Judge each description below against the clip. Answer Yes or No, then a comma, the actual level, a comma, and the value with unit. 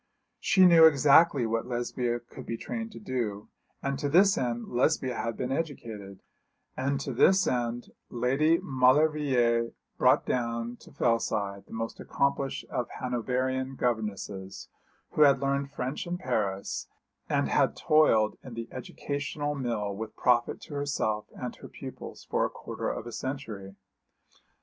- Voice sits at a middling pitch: No, low, 125 Hz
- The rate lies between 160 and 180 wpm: No, average, 145 wpm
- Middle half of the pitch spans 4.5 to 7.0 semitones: No, average, 3.4 semitones